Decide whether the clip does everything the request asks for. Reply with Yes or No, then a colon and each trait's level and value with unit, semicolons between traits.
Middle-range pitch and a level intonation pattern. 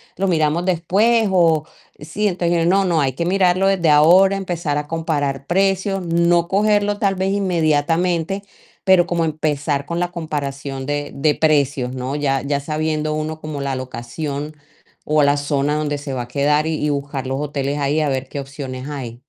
No: medium, 155 Hz; average, 3.6 semitones